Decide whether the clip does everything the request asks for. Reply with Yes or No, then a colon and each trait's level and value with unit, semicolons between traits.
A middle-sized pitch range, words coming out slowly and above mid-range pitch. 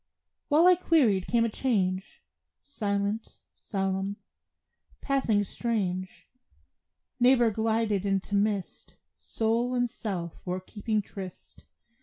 Yes: average, 3.5 semitones; slow, 100 wpm; high, 210 Hz